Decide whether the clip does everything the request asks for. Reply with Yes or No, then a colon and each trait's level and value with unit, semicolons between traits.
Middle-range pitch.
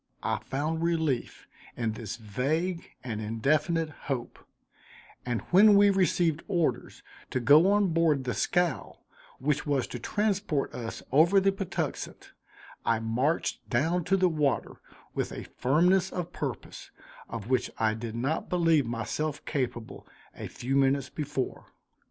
Yes: medium, 150 Hz